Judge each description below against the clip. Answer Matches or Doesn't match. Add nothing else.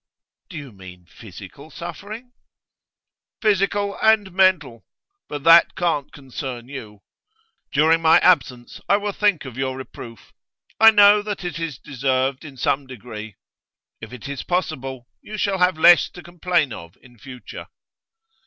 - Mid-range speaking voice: Matches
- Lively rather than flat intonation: Matches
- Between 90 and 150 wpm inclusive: Matches